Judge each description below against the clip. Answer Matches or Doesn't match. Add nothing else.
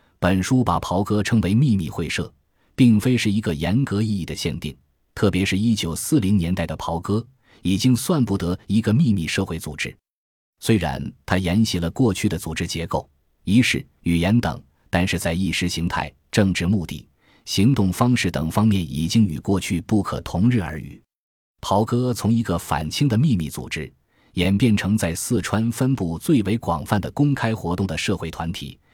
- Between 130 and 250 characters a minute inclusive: Doesn't match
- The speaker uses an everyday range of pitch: Matches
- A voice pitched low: Matches